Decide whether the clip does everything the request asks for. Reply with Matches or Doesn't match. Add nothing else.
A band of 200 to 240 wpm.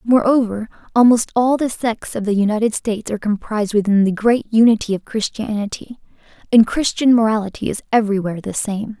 Doesn't match